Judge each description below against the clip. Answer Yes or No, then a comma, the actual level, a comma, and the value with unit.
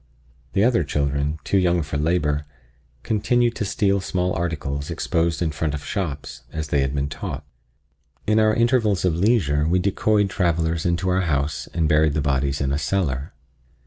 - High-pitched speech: No, very low, 80 Hz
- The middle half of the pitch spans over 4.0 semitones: Yes, average, 4.8 semitones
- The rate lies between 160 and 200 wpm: Yes, average, 175 wpm